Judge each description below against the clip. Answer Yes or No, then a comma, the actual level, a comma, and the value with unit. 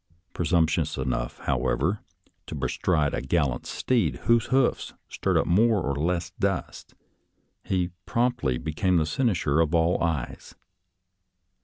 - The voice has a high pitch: No, very low, 85 Hz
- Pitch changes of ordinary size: Yes, average, 4.4 semitones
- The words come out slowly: Yes, slow, 125 wpm